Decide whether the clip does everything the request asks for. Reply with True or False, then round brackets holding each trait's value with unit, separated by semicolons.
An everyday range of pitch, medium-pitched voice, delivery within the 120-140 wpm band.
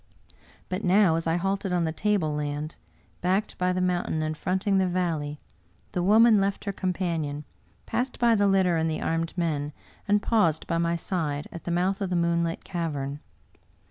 False (3.2 semitones; 175 Hz; 180 wpm)